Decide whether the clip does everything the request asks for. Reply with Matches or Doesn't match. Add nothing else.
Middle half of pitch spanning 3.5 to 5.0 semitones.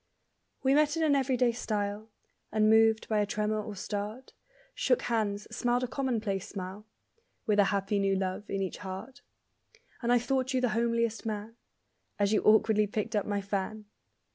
Doesn't match